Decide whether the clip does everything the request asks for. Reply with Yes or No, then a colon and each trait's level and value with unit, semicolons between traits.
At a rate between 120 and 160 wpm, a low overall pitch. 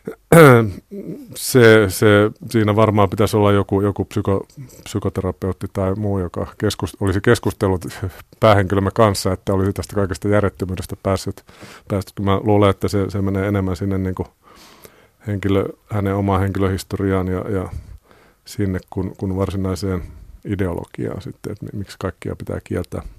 Yes: average, 130 wpm; low, 100 Hz